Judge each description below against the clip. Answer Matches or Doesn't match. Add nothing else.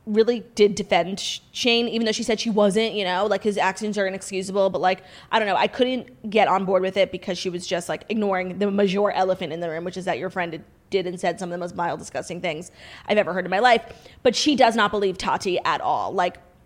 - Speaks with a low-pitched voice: Doesn't match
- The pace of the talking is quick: Matches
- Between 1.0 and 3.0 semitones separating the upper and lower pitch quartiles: Matches